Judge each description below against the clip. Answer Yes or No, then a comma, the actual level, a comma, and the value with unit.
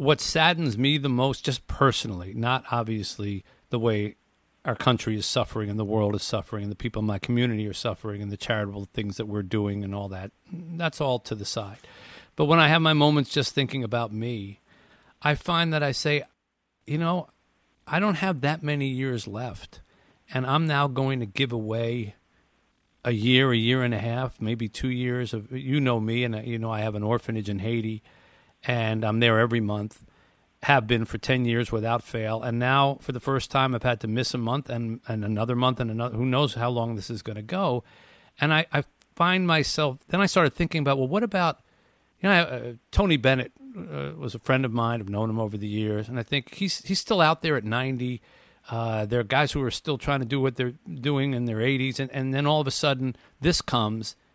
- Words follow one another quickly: Yes, fast, 220 wpm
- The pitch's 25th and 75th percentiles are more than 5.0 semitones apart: No, average, 4.1 semitones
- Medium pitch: No, low, 120 Hz